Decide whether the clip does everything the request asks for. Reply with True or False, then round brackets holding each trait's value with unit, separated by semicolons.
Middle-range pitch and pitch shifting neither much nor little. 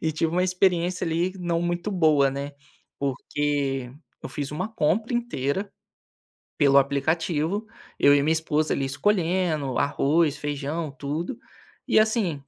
True (160 Hz; 4.1 semitones)